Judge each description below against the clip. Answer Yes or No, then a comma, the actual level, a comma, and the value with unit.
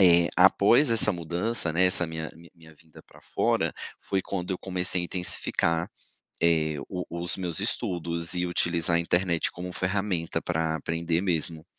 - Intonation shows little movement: Yes, narrow, 1.7 semitones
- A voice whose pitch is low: Yes, very low, 85 Hz